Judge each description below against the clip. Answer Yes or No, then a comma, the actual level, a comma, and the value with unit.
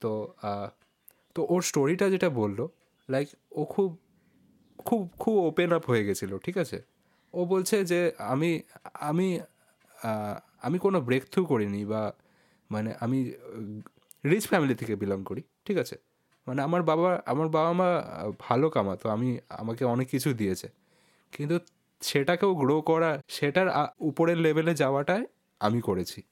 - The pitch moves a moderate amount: No, wide, 7.4 semitones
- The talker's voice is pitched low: No, medium, 150 Hz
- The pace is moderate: No, fast, 135 wpm